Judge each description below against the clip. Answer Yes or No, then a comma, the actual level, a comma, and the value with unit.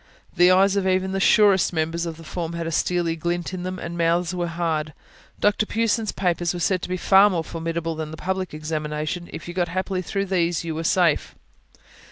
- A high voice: No, medium, 175 Hz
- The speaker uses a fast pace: Yes, fast, 215 wpm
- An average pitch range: No, narrow, 2.2 semitones